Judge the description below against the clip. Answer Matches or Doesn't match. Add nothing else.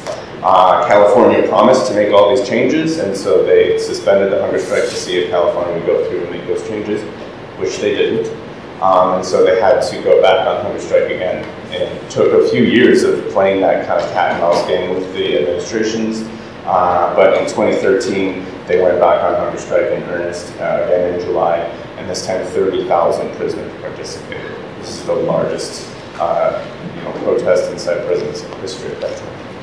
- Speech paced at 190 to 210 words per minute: Matches